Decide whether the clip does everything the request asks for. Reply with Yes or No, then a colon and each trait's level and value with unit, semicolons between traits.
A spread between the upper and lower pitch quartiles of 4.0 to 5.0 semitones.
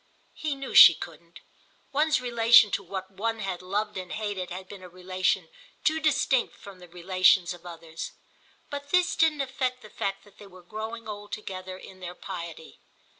Yes: average, 4.3 semitones